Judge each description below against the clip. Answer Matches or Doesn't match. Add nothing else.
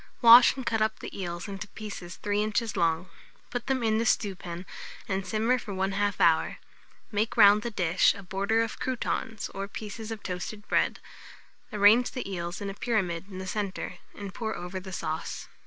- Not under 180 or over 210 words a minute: Matches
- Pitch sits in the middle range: Doesn't match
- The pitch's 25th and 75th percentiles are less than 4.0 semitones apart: Matches